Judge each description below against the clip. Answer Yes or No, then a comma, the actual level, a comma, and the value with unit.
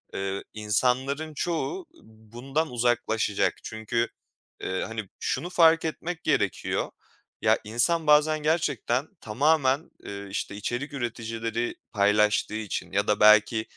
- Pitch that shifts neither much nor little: No, wide, 5.8 semitones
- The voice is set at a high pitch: No, low, 120 Hz